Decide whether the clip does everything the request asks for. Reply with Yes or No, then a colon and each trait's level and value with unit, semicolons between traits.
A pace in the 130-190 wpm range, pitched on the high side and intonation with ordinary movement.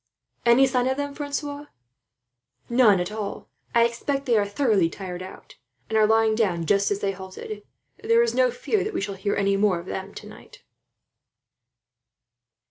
No: average, 170 wpm; high, 220 Hz; wide, 5.8 semitones